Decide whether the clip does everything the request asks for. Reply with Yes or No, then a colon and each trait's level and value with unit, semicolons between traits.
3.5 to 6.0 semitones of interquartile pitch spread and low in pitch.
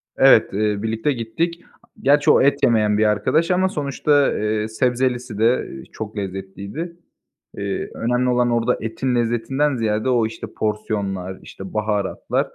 Yes: average, 3.8 semitones; low, 115 Hz